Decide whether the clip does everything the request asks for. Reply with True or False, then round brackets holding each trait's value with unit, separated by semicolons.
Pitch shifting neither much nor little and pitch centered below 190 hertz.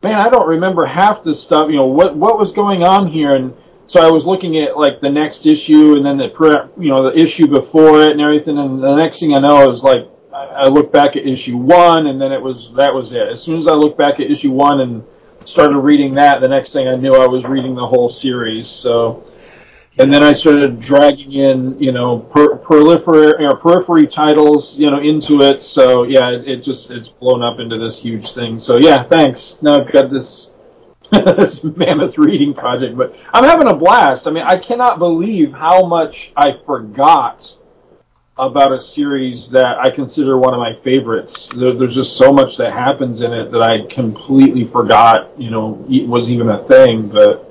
True (4.0 semitones; 140 Hz)